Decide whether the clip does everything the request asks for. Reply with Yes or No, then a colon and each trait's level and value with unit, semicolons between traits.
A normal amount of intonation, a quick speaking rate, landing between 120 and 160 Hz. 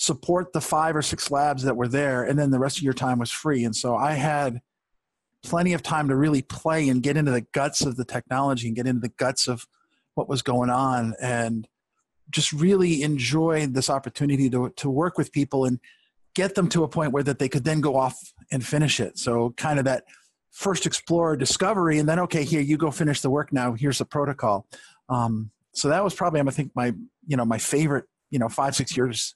Yes: average, 3.4 semitones; fast, 225 wpm; medium, 140 Hz